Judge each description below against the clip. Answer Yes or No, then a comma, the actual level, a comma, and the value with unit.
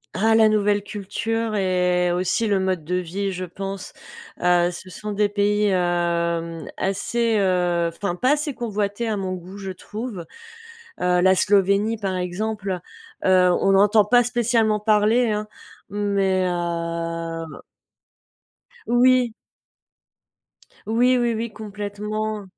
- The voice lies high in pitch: Yes, high, 200 Hz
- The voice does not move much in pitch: No, average, 3.2 semitones